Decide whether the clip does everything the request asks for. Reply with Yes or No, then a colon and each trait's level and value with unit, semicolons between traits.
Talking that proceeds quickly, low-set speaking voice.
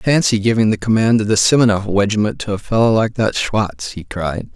Yes: fast, 210 wpm; low, 110 Hz